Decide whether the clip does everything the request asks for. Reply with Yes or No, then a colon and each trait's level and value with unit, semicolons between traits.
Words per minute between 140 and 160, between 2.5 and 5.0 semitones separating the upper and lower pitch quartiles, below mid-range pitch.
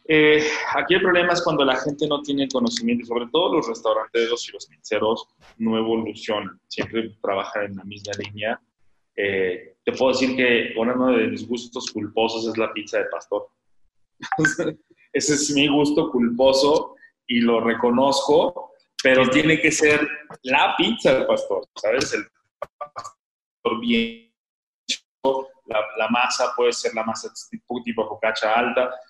No: average, 150 wpm; wide, 5.5 semitones; low, 130 Hz